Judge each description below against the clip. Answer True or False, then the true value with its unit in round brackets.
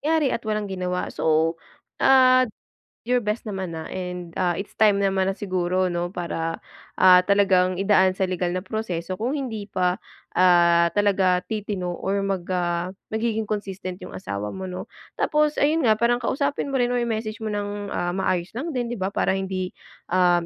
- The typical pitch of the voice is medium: False (195 Hz)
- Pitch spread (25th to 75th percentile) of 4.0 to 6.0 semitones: False (3.4 semitones)